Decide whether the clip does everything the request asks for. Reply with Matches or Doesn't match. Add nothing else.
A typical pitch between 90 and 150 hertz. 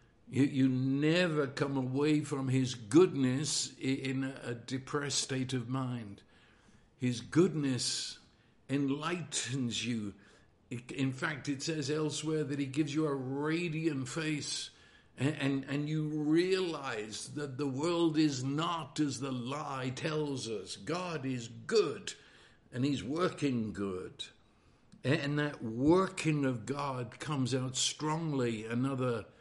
Matches